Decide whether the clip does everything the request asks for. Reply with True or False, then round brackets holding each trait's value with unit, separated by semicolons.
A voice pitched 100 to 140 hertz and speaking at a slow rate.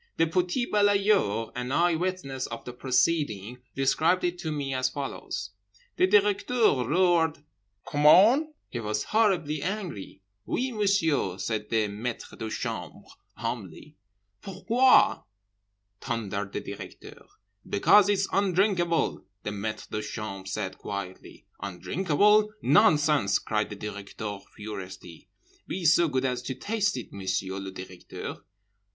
True (135 Hz; 115 wpm)